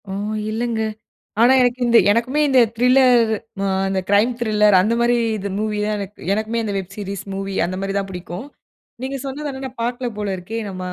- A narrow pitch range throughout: No, average, 3.5 semitones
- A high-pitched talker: Yes, high, 220 Hz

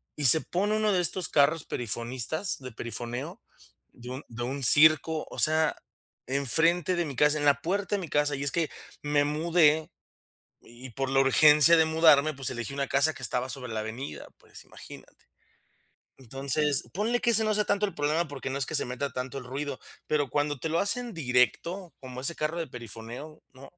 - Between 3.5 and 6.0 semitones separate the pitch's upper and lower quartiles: Yes, average, 3.8 semitones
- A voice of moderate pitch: Yes, medium, 145 Hz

